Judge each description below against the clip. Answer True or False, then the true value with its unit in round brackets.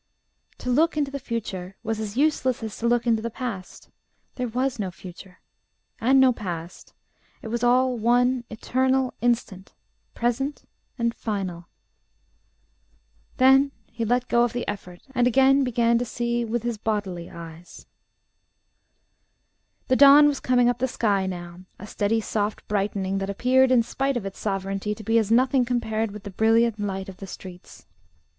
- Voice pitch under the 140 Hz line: False (230 Hz)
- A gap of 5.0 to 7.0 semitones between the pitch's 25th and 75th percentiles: False (4.0 semitones)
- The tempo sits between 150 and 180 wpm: True (160 wpm)